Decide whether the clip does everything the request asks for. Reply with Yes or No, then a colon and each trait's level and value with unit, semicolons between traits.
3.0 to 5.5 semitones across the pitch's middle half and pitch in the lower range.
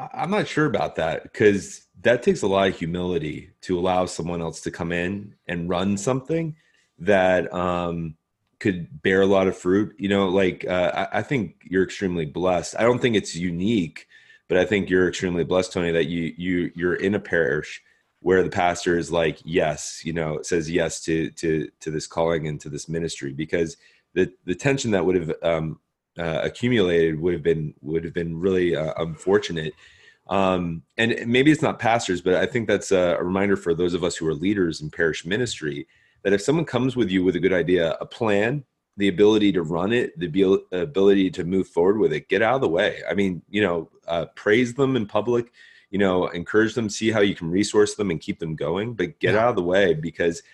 Yes: average, 3.3 semitones; very low, 95 Hz